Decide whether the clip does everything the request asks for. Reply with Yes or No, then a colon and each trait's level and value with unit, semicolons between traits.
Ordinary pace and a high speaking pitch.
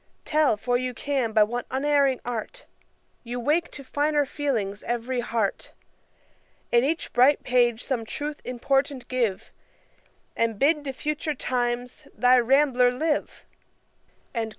No: slow, 130 wpm; very high, 255 Hz